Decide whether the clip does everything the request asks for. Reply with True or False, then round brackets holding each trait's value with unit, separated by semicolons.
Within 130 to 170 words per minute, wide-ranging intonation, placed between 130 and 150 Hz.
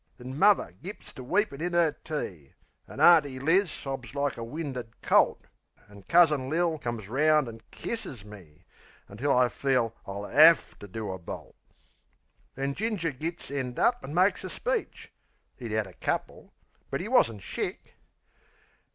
True (160 wpm; 6.3 semitones; 135 Hz)